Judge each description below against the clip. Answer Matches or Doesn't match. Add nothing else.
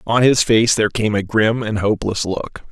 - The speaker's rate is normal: Doesn't match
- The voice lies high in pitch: Doesn't match